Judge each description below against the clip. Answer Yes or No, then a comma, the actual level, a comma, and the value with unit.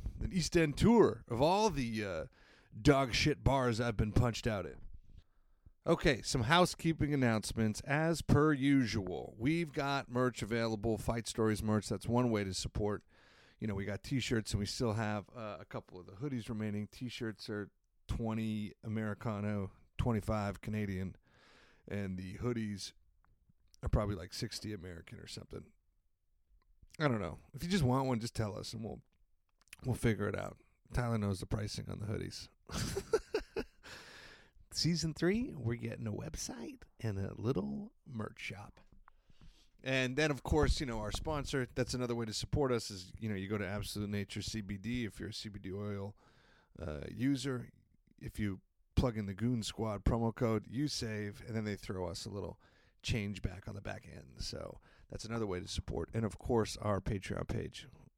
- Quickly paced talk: No, average, 175 wpm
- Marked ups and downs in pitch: No, average, 3.5 semitones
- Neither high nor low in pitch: No, low, 110 Hz